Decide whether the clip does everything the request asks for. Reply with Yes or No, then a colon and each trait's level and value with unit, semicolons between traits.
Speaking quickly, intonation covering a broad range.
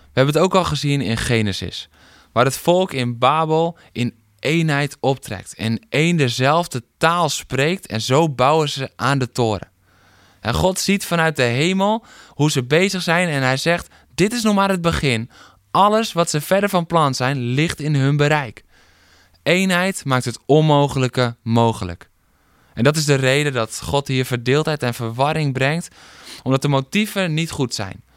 No: average, 175 wpm; wide, 6.0 semitones